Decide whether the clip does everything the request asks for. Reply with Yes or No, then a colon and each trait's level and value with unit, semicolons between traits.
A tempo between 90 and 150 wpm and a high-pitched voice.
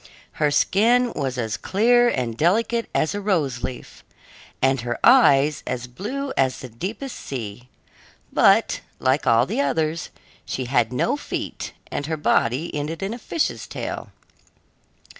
No: average, 145 wpm; medium, 145 Hz